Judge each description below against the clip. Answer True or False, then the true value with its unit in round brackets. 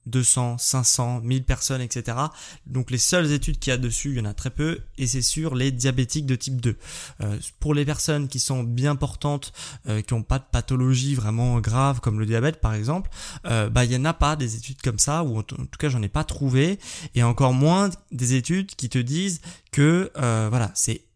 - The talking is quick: True (225 wpm)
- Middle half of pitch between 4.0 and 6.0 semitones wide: False (3.3 semitones)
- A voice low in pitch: True (130 Hz)